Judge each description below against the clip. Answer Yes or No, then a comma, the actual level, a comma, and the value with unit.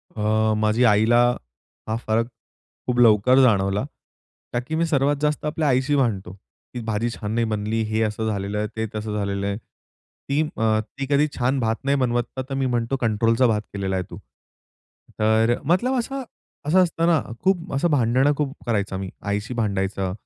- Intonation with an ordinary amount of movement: Yes, average, 4.3 semitones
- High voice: No, low, 115 Hz